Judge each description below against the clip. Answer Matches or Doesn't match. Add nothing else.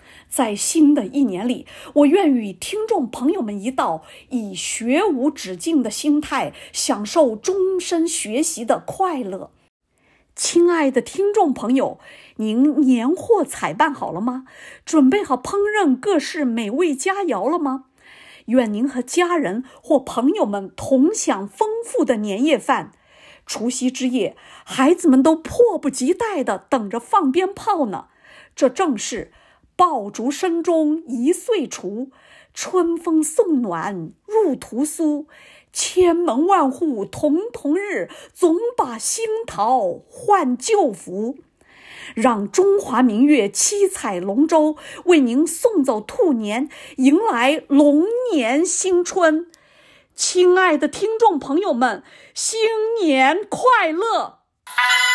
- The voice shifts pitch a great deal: Matches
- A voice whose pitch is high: Matches